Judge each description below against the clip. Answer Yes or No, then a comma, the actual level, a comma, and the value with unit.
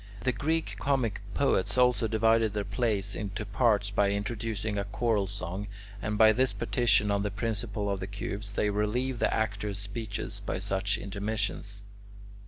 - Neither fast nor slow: Yes, average, 160 wpm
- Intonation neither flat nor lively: No, narrow, 2.1 semitones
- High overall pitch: No, low, 105 Hz